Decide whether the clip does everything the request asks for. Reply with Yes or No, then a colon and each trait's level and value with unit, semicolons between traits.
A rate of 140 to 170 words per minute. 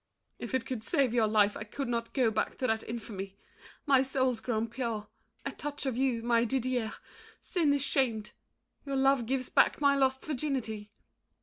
No: average, 180 wpm